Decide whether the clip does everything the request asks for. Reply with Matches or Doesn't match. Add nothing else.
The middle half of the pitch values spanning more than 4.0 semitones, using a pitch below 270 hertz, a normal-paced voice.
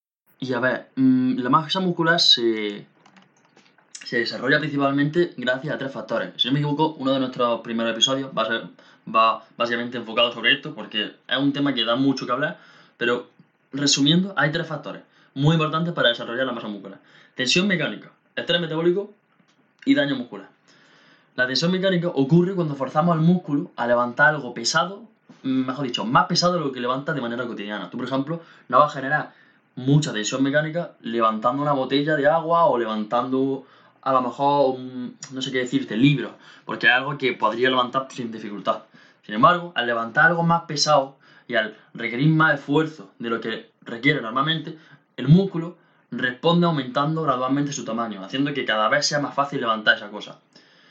Matches